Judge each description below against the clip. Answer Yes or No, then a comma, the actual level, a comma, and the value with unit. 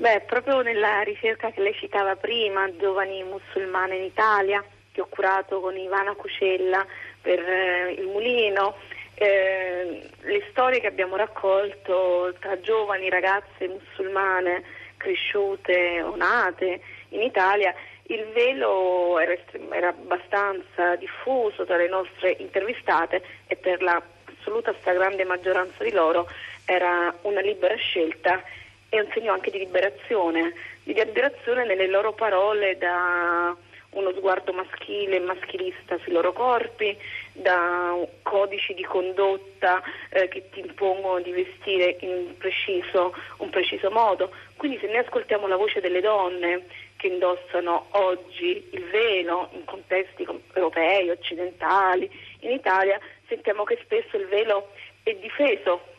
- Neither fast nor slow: Yes, average, 130 wpm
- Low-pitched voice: No, high, 195 Hz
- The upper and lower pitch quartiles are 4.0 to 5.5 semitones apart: No, average, 3.1 semitones